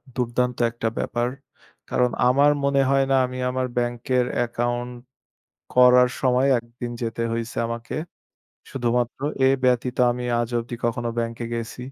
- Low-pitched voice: Yes, low, 120 Hz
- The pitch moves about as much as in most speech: No, narrow, 1.2 semitones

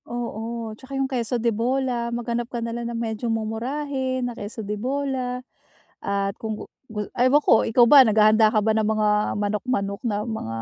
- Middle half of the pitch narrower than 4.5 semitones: Yes, narrow, 2.6 semitones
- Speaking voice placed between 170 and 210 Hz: No, high, 230 Hz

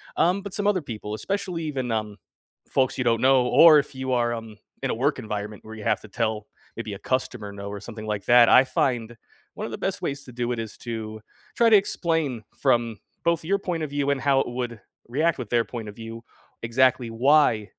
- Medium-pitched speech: No, low, 120 Hz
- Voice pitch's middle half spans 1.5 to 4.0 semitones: No, average, 4.4 semitones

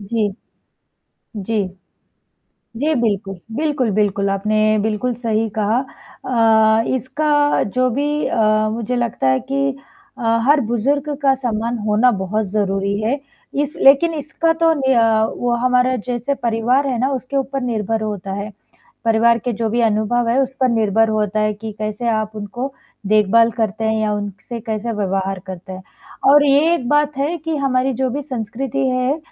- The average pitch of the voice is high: Yes, high, 230 Hz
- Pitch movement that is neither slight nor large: Yes, average, 3.9 semitones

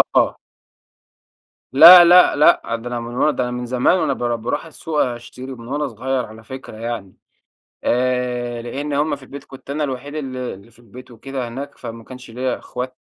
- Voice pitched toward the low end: Yes, low, 125 Hz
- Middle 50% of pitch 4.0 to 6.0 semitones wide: No, average, 2.8 semitones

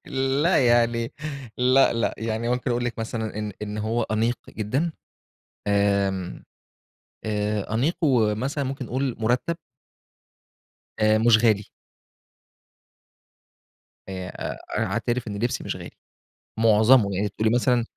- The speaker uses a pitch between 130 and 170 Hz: No, low, 115 Hz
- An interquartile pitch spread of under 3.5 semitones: Yes, average, 2.8 semitones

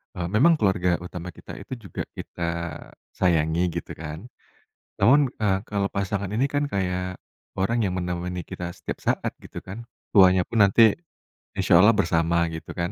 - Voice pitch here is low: Yes, very low, 95 Hz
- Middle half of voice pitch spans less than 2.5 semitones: No, average, 2.9 semitones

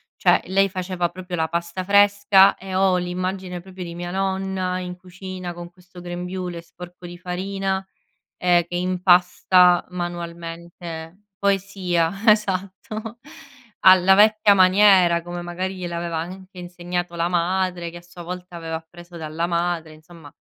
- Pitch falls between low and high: Yes, medium, 180 Hz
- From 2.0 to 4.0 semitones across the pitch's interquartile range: No, narrow, 1.6 semitones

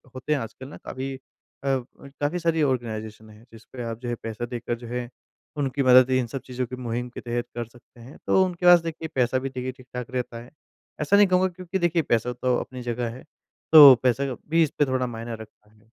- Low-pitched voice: Yes, low, 125 Hz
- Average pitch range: Yes, average, 3.2 semitones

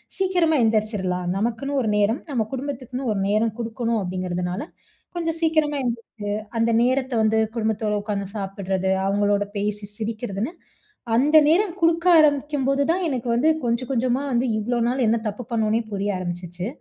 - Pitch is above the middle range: Yes, high, 230 Hz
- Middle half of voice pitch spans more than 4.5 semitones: Yes, average, 5.1 semitones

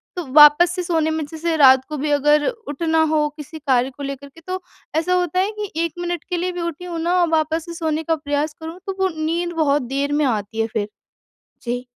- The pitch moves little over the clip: No, average, 3.1 semitones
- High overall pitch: Yes, very high, 315 Hz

